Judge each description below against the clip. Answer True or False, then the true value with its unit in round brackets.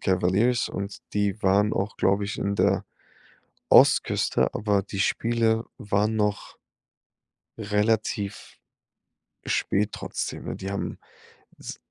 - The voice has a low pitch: True (105 Hz)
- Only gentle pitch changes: True (1.6 semitones)